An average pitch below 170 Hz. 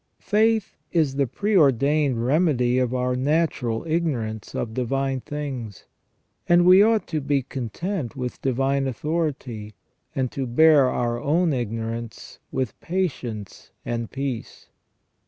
Yes: low, 135 Hz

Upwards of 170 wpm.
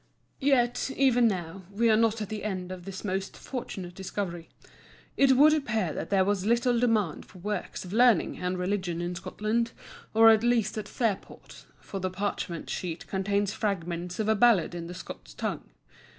Yes: average, 180 wpm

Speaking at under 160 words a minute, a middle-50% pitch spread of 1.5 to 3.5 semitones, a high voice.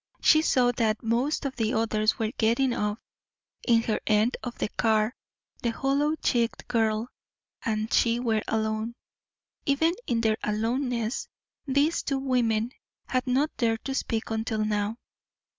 Yes: average, 145 wpm; average, 2.7 semitones; high, 230 Hz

